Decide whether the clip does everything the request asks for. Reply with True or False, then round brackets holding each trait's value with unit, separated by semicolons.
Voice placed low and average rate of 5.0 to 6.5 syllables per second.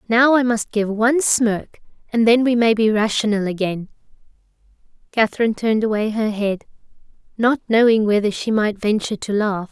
False (220 Hz; 5.3 syllables/s)